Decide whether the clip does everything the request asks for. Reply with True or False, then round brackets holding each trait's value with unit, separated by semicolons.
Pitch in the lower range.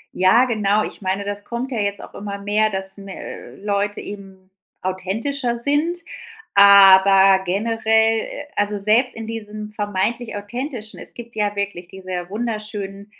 False (205 Hz)